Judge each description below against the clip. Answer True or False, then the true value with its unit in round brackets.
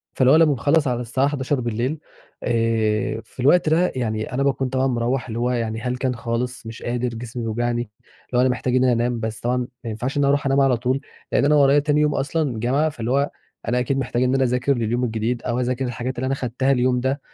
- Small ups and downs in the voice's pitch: True (2.3 semitones)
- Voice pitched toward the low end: True (125 Hz)